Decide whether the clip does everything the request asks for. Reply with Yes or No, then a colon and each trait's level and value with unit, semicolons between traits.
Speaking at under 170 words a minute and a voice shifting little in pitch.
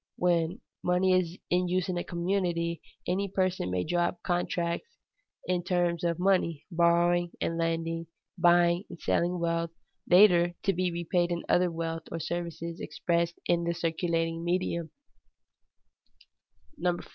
Yes: slow, 135 wpm; narrow, 1.1 semitones